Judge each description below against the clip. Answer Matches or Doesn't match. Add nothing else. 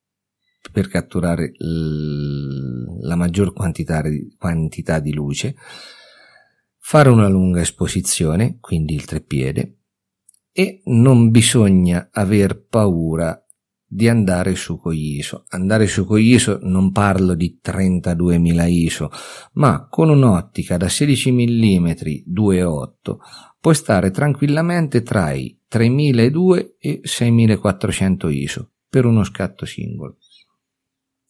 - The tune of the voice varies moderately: Doesn't match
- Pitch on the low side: Matches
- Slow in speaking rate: Matches